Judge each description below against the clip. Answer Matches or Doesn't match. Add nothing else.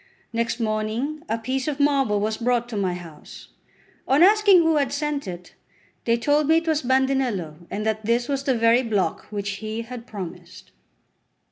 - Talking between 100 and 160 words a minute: Doesn't match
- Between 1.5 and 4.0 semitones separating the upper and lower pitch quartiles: Doesn't match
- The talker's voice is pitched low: Doesn't match